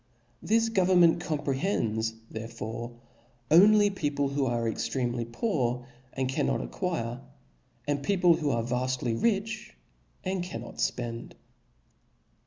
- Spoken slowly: Yes, slow, 115 wpm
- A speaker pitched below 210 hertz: Yes, low, 135 Hz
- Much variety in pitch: Yes, wide, 7.5 semitones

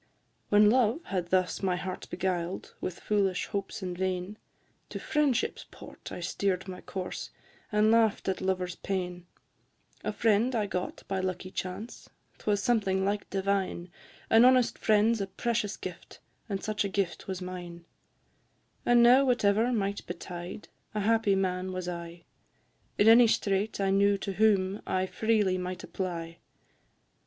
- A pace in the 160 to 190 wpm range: No, average, 150 wpm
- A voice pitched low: No, high, 195 Hz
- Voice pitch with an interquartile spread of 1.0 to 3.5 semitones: Yes, average, 2.7 semitones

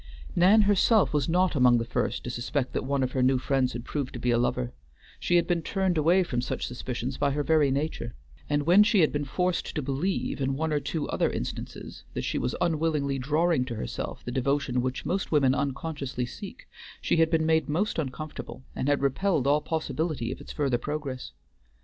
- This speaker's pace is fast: Yes, fast, 210 wpm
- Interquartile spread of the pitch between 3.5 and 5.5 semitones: Yes, average, 4.1 semitones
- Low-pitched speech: No, medium, 145 Hz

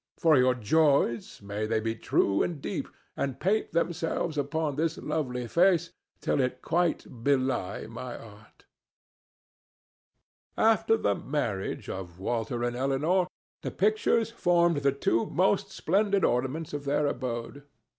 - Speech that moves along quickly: No, slow, 135 wpm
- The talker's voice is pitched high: No, medium, 140 Hz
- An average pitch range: No, wide, 6.1 semitones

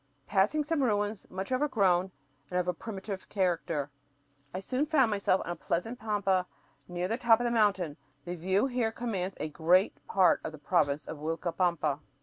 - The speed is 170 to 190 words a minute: Yes, average, 180 wpm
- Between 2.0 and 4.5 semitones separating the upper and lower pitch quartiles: Yes, average, 4.2 semitones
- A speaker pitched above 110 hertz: Yes, high, 190 Hz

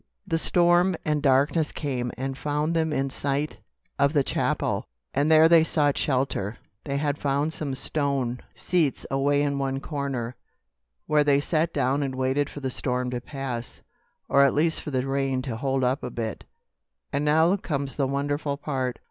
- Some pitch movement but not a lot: No, narrow, 2.2 semitones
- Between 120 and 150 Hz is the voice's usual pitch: Yes, medium, 140 Hz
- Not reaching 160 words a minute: No, average, 175 wpm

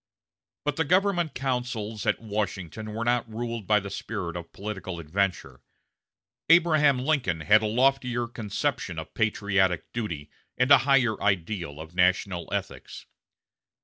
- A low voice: Yes, low, 110 Hz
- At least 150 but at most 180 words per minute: No, slow, 135 wpm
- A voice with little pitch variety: No, average, 5.0 semitones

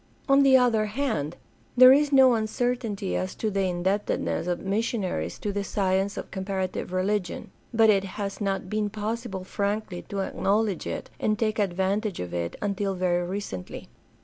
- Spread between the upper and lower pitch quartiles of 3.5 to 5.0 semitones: No, average, 2.7 semitones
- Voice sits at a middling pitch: No, high, 200 Hz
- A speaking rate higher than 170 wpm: No, average, 165 wpm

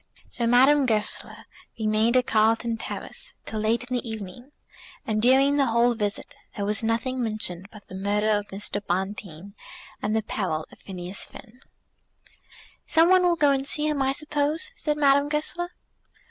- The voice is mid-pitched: No, high, 230 Hz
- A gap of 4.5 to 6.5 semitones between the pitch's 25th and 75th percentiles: Yes, average, 4.9 semitones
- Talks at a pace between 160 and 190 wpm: Yes, average, 165 wpm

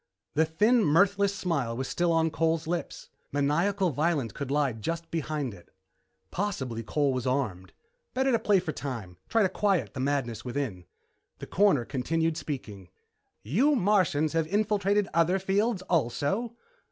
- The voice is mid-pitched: Yes, medium, 160 Hz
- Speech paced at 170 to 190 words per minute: No, average, 150 wpm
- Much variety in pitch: Yes, wide, 6.7 semitones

